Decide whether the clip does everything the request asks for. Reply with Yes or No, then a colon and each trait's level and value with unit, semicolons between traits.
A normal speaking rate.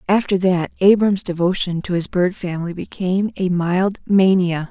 Yes: average, 155 wpm